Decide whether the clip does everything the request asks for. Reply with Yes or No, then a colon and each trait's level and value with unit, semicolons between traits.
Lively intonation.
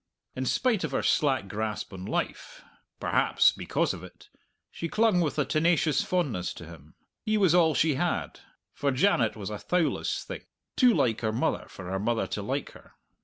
Yes: wide, 8.5 semitones